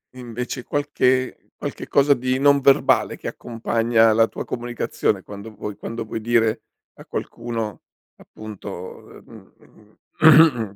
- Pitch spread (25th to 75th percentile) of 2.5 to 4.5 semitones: Yes, average, 2.9 semitones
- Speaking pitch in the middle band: No, low, 115 Hz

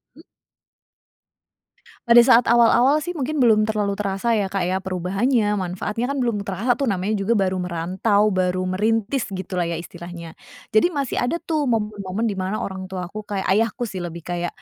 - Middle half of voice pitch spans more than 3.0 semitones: Yes, average, 4.0 semitones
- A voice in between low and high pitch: No, high, 205 Hz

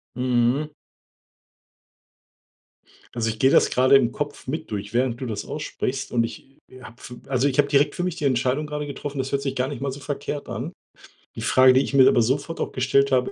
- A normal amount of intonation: No, narrow, 2.2 semitones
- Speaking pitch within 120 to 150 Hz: Yes, low, 135 Hz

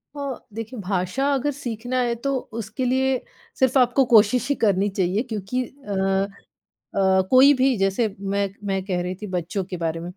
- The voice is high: Yes, high, 215 Hz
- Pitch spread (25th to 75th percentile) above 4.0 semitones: Yes, average, 5.0 semitones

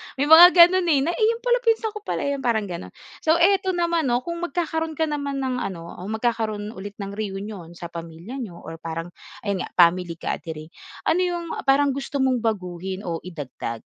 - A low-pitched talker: No, high, 240 Hz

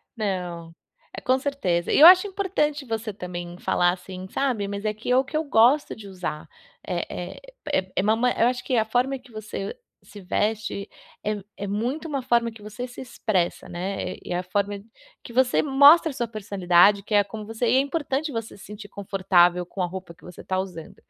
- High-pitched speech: Yes, high, 215 Hz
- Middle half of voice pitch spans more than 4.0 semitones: Yes, average, 5.2 semitones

